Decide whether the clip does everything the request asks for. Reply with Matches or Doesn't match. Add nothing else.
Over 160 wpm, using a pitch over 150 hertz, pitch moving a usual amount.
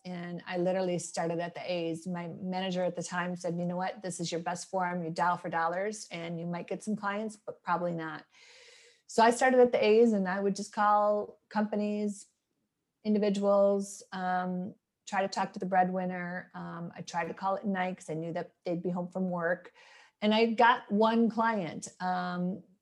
Matches